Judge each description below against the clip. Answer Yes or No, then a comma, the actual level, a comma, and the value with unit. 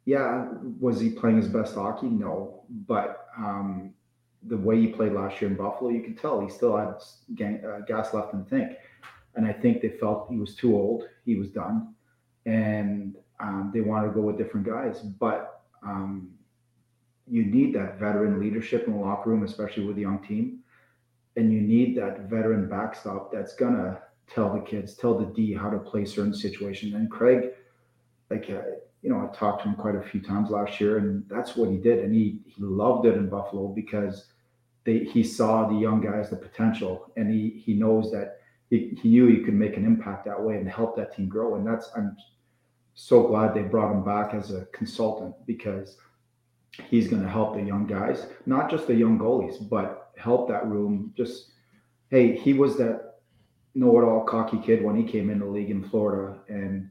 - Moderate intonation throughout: Yes, average, 3.0 semitones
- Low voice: Yes, low, 110 Hz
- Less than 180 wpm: No, average, 200 wpm